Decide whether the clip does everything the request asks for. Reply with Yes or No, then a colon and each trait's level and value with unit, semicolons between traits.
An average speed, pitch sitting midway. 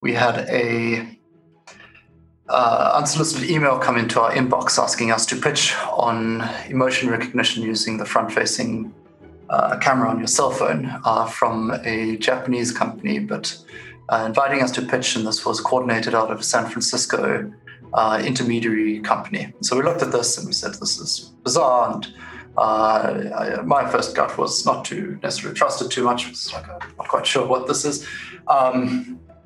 No: average, 170 wpm; low, 115 Hz